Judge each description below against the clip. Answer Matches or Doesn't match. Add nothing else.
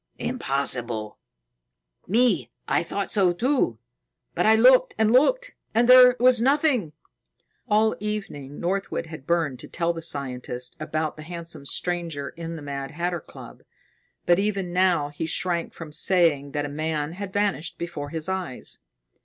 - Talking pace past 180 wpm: Doesn't match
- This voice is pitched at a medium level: Matches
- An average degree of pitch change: Doesn't match